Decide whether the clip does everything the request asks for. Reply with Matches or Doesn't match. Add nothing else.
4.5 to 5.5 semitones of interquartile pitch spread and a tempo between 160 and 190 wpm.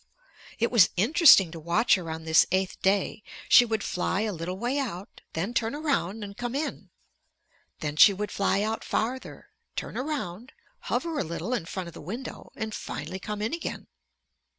Matches